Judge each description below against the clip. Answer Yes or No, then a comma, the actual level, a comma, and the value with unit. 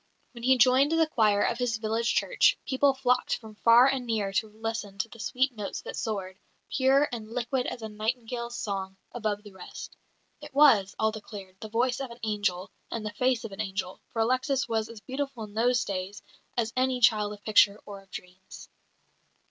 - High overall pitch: Yes, high, 225 Hz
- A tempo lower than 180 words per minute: No, average, 195 wpm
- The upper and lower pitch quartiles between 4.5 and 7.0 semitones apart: No, average, 3.3 semitones